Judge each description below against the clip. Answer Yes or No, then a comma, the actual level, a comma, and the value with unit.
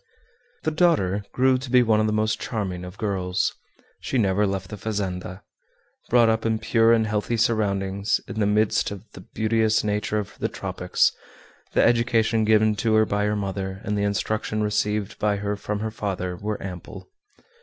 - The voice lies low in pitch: Yes, low, 105 Hz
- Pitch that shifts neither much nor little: No, narrow, 1.8 semitones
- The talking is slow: No, average, 180 wpm